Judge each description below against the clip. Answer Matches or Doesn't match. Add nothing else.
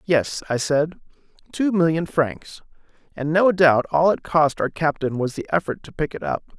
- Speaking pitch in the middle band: Matches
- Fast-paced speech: Doesn't match